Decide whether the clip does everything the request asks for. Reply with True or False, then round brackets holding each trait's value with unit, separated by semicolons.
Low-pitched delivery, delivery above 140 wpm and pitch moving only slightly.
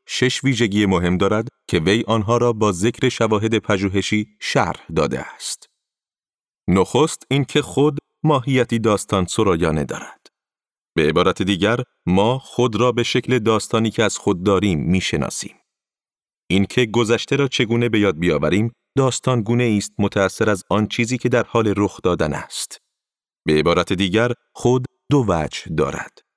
False (115 Hz; 150 wpm; 3.8 semitones)